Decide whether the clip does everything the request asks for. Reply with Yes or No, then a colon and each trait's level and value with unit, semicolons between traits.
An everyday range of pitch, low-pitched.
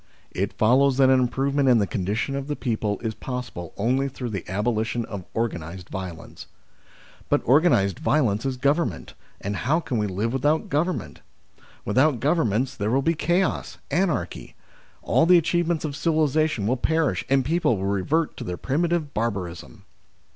No: wide, 6.4 semitones; low, 130 Hz